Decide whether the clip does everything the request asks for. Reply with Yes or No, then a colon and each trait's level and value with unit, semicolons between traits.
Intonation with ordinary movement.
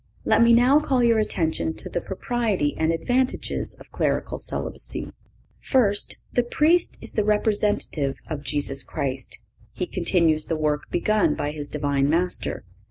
No: wide, 7.6 semitones